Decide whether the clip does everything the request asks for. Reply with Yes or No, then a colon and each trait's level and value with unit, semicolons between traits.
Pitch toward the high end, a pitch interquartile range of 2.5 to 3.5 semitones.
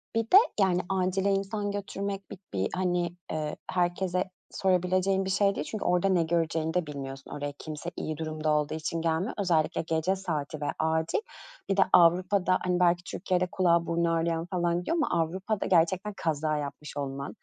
No: medium, 175 Hz; average, 3.0 semitones